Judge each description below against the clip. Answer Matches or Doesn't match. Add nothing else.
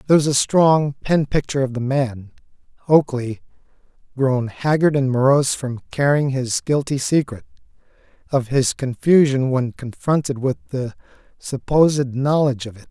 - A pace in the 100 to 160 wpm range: Matches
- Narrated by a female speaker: Doesn't match